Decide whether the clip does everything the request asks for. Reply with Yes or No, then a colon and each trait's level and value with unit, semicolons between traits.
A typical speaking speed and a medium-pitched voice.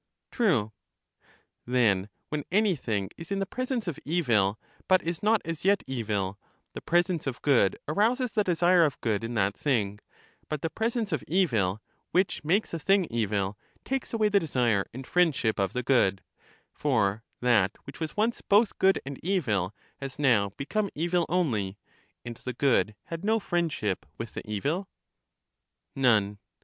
Yes: average, 160 wpm; medium, 145 Hz